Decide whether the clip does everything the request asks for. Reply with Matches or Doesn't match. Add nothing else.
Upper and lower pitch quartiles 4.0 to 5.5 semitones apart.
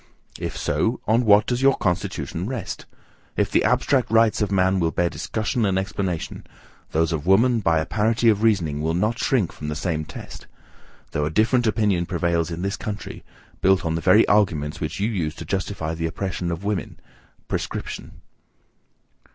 Matches